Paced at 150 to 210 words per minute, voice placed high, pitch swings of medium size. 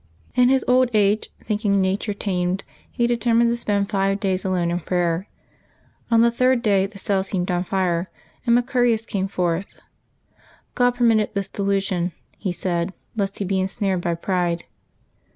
Yes: average, 160 wpm; high, 195 Hz; average, 3.7 semitones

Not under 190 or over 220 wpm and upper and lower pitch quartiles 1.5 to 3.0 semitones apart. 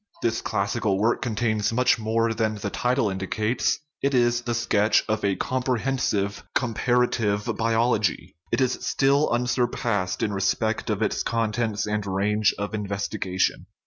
No: average, 145 wpm; average, 2.7 semitones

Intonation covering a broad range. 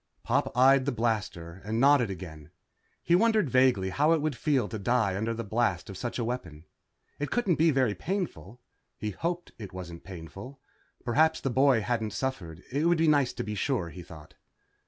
Yes: wide, 6.7 semitones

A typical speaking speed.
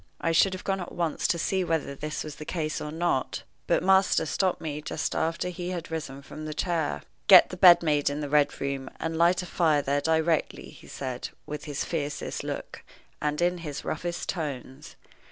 No: fast, 210 wpm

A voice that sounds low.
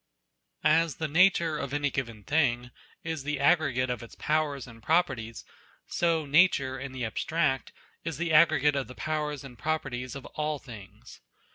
No: medium, 145 Hz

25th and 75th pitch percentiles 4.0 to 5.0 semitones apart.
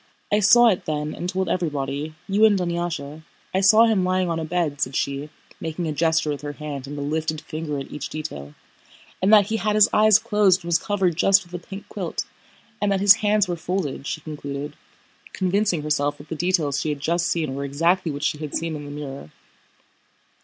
Yes: average, 4.5 semitones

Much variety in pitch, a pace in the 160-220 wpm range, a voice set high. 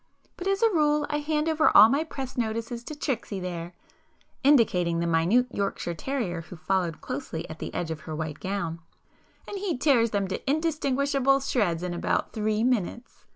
Yes: wide, 8.3 semitones; average, 170 wpm; high, 230 Hz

